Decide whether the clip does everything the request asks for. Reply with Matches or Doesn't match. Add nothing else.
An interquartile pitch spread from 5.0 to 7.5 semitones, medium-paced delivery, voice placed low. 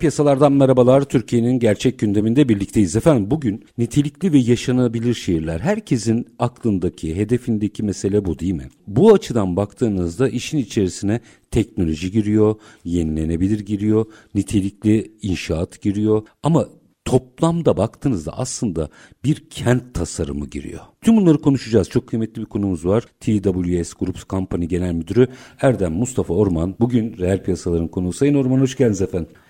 Matches